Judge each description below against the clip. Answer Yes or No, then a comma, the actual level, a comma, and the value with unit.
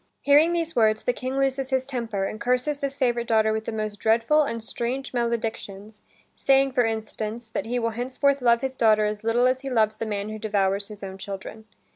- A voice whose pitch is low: No, high, 230 Hz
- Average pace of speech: No, fast, 210 wpm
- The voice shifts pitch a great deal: No, average, 3.2 semitones